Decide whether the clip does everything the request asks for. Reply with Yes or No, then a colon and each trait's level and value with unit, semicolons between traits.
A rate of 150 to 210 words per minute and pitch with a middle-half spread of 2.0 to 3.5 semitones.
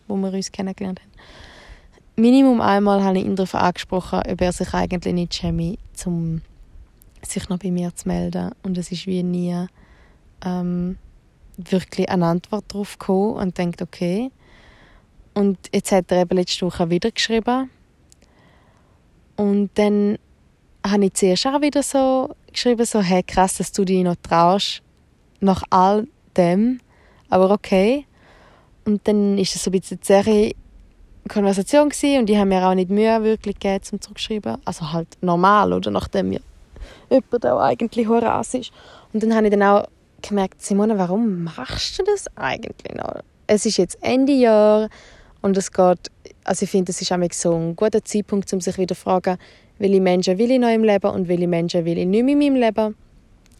Yes: average, 175 wpm; average, 2.9 semitones